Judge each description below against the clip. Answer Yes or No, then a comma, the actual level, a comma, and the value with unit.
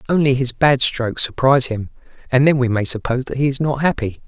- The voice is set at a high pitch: No, low, 130 Hz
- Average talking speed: No, fast, 225 wpm